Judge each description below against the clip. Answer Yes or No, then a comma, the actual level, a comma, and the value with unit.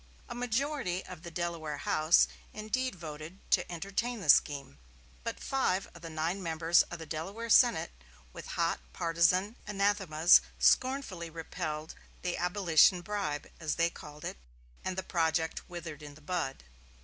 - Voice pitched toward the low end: No, medium, 175 Hz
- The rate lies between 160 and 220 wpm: No, average, 150 wpm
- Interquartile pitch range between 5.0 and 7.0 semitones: No, average, 4.1 semitones